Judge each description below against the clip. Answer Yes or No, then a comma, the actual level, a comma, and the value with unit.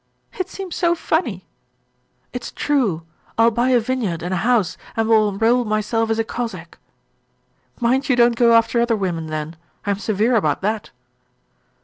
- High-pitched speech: Yes, high, 225 Hz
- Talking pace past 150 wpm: Yes, average, 170 wpm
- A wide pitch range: No, average, 3.6 semitones